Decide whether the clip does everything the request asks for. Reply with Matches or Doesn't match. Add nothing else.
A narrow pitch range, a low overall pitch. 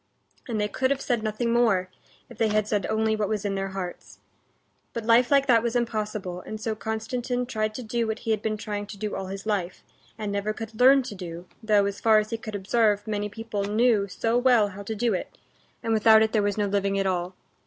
Doesn't match